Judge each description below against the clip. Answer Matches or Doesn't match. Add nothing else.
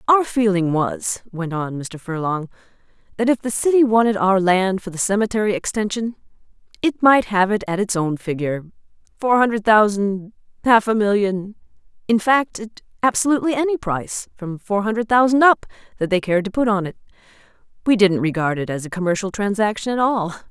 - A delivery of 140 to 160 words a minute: Doesn't match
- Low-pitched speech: Doesn't match